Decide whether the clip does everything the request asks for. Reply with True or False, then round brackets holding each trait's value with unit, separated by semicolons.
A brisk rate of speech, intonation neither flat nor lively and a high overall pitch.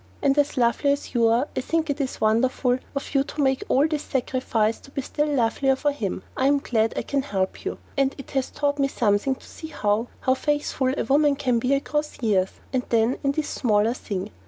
True (225 wpm; 3.6 semitones; 265 Hz)